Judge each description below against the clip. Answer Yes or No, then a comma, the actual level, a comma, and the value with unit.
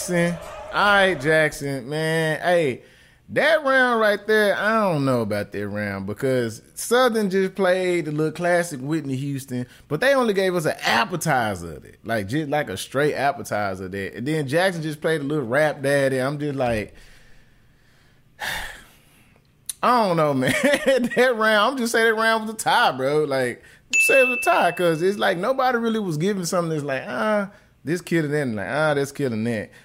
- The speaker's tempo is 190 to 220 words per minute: Yes, average, 195 wpm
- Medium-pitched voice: Yes, medium, 160 Hz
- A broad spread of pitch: Yes, wide, 7.6 semitones